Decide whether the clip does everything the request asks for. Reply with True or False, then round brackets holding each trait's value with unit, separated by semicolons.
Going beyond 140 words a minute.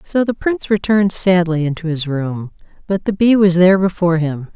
True (200 wpm)